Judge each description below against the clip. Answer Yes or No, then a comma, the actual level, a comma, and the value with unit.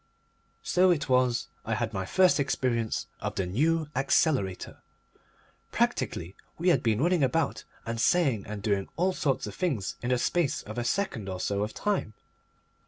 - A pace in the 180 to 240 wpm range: No, average, 170 wpm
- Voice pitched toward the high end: No, low, 125 Hz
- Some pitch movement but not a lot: No, wide, 7.5 semitones